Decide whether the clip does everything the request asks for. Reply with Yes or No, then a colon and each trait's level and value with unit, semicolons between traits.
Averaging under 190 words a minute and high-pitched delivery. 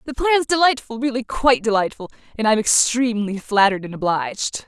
Yes: average, 140 wpm; high, 230 Hz